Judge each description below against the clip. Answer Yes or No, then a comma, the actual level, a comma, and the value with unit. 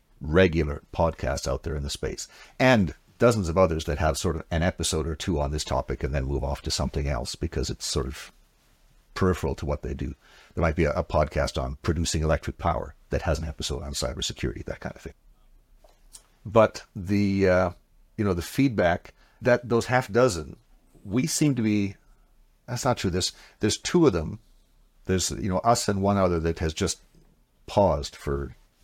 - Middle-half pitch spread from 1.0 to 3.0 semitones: No, average, 4.9 semitones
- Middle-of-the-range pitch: No, very low, 85 Hz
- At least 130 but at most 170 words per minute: No, average, 200 wpm